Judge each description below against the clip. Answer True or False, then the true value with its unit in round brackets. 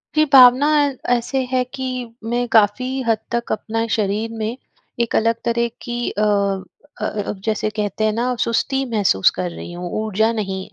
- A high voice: True (230 Hz)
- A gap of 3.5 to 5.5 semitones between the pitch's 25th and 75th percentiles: False (2.5 semitones)